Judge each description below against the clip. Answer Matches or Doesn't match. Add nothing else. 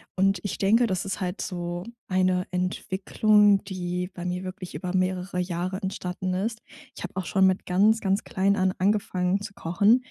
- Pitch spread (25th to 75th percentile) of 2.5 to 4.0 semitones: Doesn't match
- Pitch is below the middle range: Doesn't match